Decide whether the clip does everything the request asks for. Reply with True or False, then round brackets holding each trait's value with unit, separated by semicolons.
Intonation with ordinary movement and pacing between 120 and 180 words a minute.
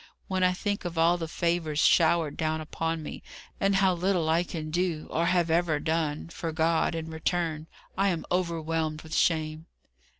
False (1.8 semitones; 175 wpm)